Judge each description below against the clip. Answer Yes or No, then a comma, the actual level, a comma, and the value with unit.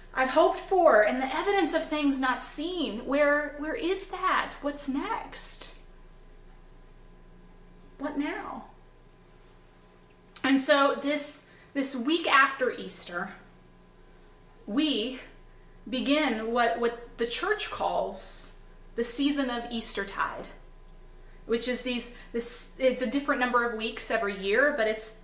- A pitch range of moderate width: No, wide, 6.0 semitones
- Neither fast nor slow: No, slow, 120 wpm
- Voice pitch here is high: Yes, very high, 250 Hz